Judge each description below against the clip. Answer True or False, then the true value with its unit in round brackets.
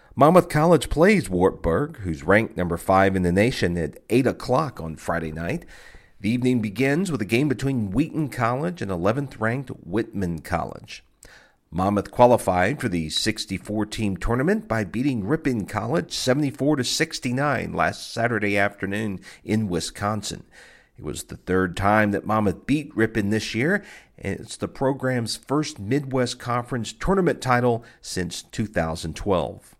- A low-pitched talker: True (110 Hz)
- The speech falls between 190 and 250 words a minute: False (145 wpm)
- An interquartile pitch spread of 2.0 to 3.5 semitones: False (5.4 semitones)